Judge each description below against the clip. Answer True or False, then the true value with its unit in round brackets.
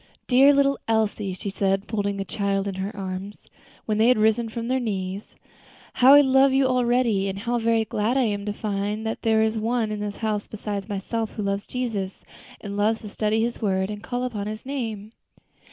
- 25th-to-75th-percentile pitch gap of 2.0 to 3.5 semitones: True (2.9 semitones)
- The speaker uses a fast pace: True (210 wpm)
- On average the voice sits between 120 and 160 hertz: False (215 Hz)